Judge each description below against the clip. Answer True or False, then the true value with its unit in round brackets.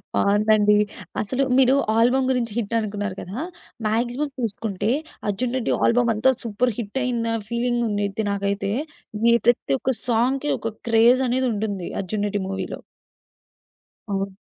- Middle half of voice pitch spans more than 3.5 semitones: False (3.2 semitones)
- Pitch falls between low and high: False (225 Hz)